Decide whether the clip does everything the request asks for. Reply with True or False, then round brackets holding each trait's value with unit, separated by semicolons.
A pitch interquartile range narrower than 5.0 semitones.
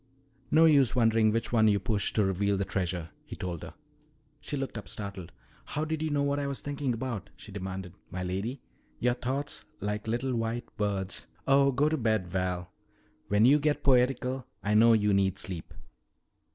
False (5.4 semitones)